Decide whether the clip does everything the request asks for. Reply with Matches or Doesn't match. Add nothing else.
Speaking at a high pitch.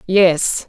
Doesn't match